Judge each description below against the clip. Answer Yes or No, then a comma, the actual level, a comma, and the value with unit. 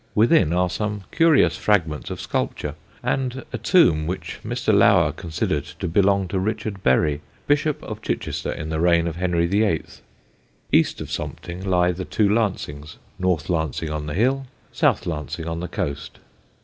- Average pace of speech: Yes, average, 160 wpm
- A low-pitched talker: Yes, very low, 90 Hz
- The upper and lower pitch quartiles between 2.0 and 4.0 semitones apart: No, average, 4.7 semitones